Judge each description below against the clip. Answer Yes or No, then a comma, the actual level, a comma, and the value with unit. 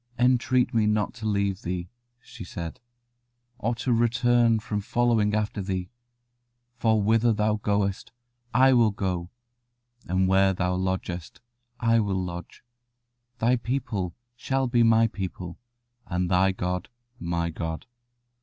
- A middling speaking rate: No, slow, 130 wpm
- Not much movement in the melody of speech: No, average, 4.1 semitones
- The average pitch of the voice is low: Yes, low, 105 Hz